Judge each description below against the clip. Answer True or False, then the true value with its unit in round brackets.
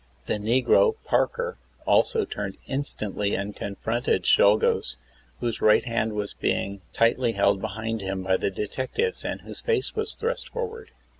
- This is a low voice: True (115 Hz)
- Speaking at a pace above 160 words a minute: False (145 wpm)